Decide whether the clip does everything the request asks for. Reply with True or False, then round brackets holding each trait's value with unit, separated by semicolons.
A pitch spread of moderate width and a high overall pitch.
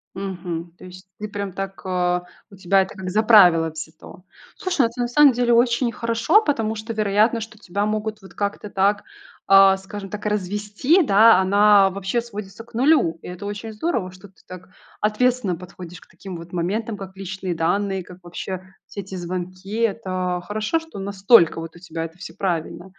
True (3.0 semitones; 195 Hz)